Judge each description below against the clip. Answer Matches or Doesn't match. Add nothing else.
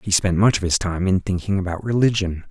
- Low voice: Matches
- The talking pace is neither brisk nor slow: Doesn't match